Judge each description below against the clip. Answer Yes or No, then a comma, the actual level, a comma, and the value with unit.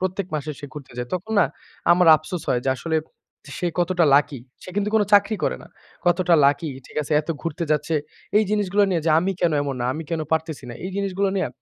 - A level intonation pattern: No, average, 3.7 semitones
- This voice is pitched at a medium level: Yes, medium, 170 Hz